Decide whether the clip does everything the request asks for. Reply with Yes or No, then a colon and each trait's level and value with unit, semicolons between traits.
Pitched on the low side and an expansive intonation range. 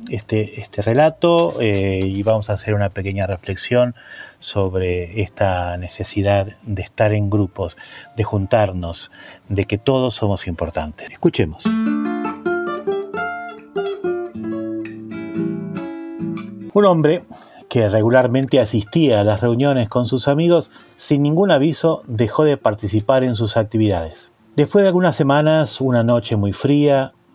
Yes: low, 115 Hz; wide, 6.5 semitones